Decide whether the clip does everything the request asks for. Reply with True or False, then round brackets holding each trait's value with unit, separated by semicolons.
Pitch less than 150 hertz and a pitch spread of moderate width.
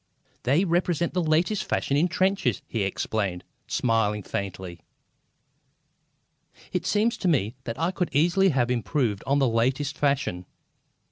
False (140 Hz; 7.6 semitones)